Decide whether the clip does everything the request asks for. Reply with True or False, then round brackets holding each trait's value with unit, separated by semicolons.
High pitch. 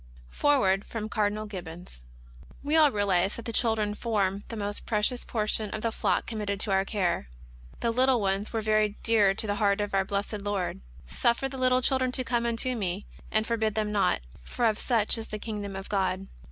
True (210 Hz)